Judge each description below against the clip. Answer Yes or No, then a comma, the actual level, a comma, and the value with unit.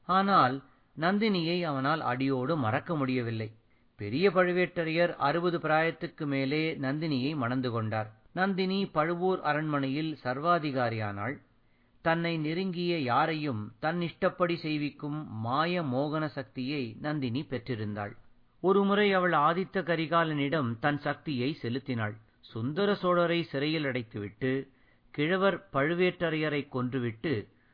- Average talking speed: Yes, average, 95 wpm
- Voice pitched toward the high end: No, medium, 150 Hz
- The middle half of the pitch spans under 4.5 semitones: No, average, 4.9 semitones